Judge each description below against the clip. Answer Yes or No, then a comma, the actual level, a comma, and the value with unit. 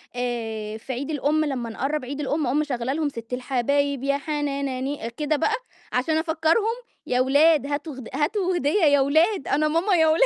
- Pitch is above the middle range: Yes, very high, 285 Hz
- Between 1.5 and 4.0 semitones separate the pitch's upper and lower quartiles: Yes, average, 3.3 semitones